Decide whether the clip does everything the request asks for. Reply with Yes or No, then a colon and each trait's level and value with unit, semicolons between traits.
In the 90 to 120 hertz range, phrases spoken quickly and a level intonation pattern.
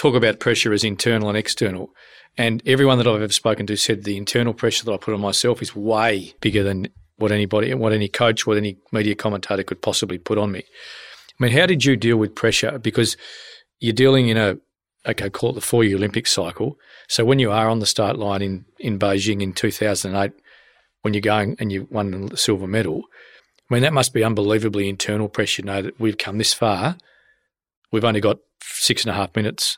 Yes: low, 105 Hz; fast, 215 wpm; narrow, 2.1 semitones